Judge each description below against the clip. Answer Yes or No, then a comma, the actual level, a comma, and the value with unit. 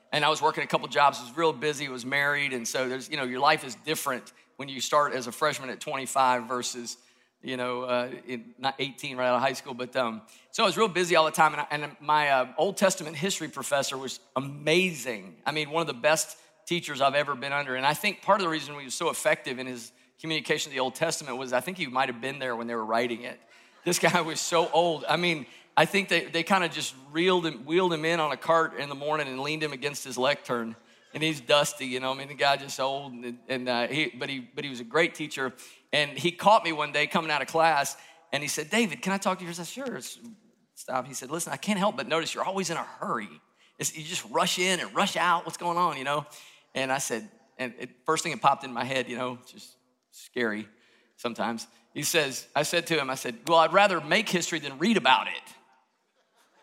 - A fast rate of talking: Yes, fast, 255 wpm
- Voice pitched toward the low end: No, medium, 145 Hz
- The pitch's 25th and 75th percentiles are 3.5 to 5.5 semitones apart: Yes, average, 4.2 semitones